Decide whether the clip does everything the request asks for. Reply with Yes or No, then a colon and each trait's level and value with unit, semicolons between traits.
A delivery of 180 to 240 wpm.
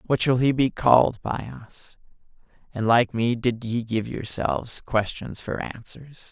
No: average, 160 wpm